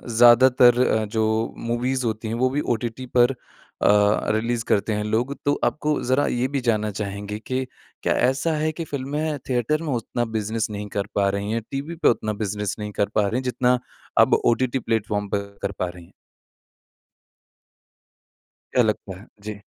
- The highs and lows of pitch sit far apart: No, average, 3.6 semitones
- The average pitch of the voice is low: Yes, low, 115 Hz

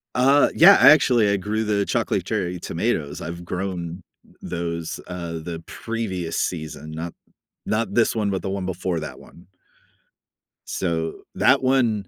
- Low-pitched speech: Yes, very low, 95 Hz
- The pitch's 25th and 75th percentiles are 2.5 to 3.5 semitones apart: No, average, 4.6 semitones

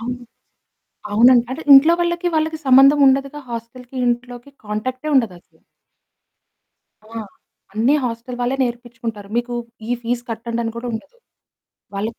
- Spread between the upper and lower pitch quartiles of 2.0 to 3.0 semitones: Yes, average, 2.7 semitones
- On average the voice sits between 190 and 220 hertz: No, high, 245 Hz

